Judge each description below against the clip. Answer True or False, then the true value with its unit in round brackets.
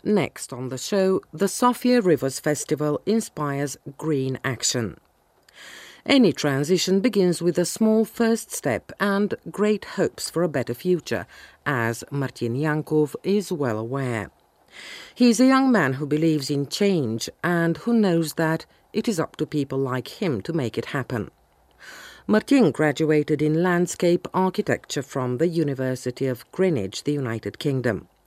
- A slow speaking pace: False (145 wpm)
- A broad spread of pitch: True (6.0 semitones)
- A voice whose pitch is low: False (155 Hz)